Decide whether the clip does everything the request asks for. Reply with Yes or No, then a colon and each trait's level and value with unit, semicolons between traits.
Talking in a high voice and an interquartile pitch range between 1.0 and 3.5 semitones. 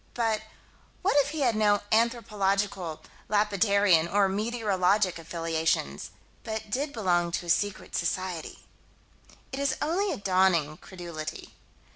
No: high, 200 Hz; average, 4.1 semitones